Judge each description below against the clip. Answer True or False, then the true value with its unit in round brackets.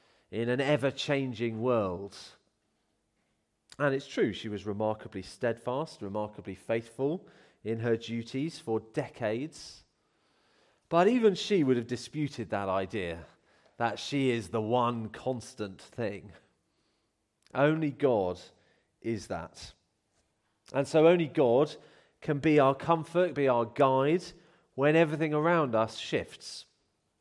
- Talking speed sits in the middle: False (120 wpm)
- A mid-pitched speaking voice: False (125 Hz)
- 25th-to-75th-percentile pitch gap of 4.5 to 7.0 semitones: True (5.1 semitones)